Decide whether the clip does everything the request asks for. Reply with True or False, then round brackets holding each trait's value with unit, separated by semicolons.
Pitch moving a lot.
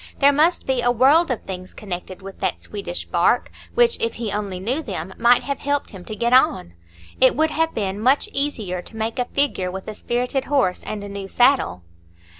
True (6.1 semitones)